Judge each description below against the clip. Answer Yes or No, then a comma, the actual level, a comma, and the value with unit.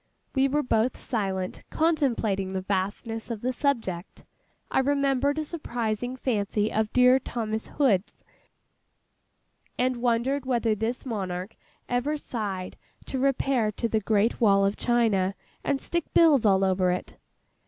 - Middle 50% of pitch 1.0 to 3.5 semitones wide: No, average, 4.7 semitones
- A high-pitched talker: Yes, high, 230 Hz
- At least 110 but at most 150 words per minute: Yes, slow, 135 wpm